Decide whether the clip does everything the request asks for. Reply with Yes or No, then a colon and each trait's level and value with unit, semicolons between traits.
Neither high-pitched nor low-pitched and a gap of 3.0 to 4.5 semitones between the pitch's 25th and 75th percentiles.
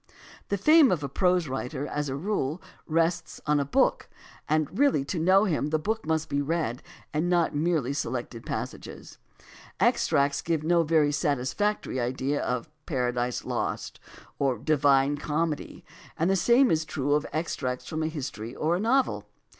Yes: medium, 155 Hz; average, 3.6 semitones